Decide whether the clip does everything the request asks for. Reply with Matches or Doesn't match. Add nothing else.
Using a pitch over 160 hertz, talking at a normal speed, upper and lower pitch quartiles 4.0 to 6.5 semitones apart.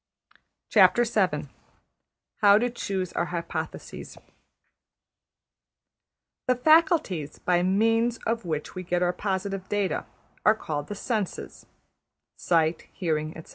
Doesn't match